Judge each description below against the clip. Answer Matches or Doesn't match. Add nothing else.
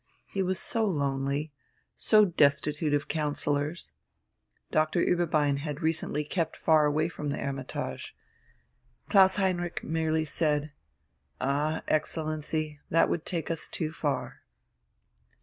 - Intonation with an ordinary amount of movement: Doesn't match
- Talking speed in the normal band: Doesn't match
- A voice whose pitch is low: Doesn't match